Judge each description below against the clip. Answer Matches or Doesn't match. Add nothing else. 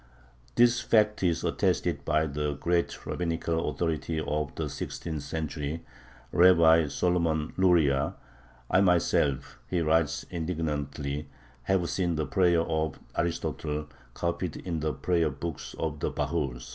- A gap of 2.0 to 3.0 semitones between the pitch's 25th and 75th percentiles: Matches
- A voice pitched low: Matches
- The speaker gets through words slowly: Matches